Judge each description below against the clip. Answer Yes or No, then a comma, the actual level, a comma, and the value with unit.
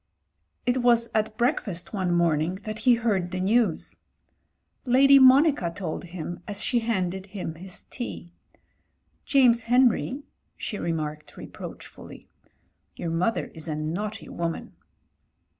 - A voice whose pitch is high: Yes, high, 200 Hz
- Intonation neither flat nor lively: No, wide, 5.7 semitones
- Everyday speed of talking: No, slow, 125 wpm